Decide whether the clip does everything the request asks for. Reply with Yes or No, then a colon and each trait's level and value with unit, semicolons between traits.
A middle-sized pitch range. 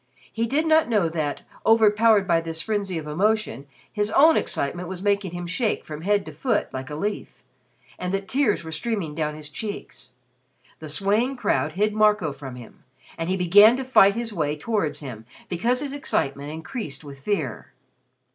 No: wide, 6.0 semitones